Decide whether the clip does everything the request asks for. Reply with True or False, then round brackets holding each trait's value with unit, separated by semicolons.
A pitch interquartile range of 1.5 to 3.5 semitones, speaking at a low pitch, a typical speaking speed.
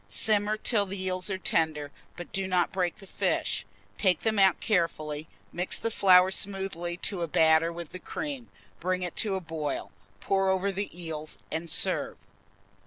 False (2.7 semitones; 185 Hz; 175 wpm)